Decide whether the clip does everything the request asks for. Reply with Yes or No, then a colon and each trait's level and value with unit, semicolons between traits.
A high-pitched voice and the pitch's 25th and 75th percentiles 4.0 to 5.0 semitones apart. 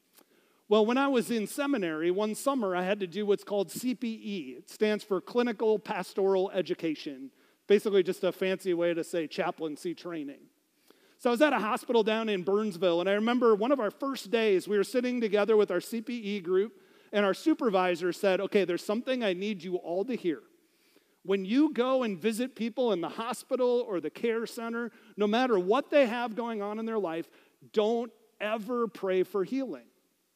Yes: high, 215 Hz; average, 4.3 semitones